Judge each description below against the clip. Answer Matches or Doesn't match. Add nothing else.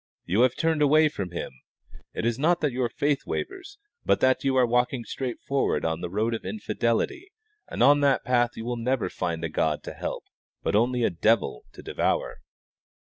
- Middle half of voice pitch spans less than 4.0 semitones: Doesn't match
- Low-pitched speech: Matches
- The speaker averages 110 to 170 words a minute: Doesn't match